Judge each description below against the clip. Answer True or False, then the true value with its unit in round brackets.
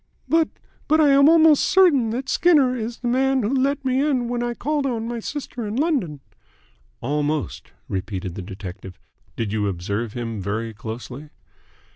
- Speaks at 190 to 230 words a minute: False (165 wpm)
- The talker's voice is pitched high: True (235 Hz)